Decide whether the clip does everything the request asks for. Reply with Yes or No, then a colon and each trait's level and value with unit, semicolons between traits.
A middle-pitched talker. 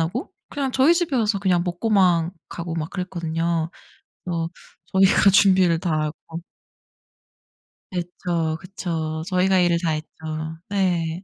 Yes: medium, 175 Hz